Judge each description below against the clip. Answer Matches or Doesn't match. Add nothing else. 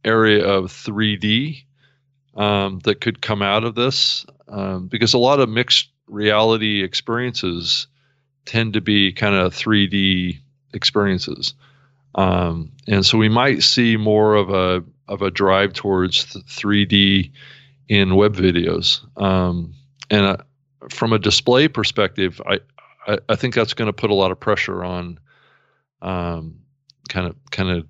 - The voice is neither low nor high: Doesn't match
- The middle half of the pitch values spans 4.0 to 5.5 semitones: Matches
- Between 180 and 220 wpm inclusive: Doesn't match